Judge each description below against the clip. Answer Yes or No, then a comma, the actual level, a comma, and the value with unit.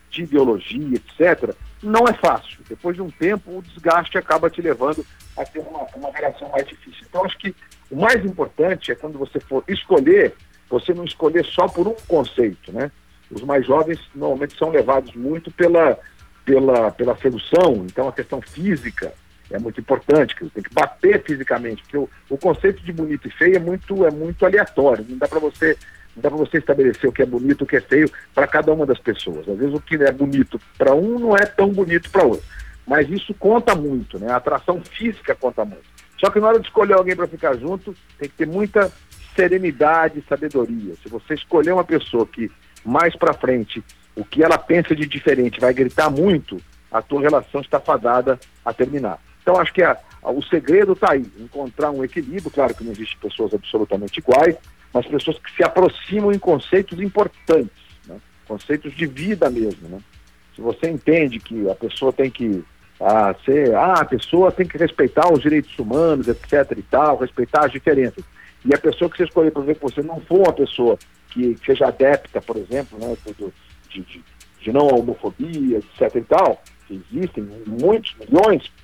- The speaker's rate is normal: No, fast, 195 wpm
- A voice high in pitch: No, medium, 150 Hz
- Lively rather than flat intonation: Yes, wide, 6.3 semitones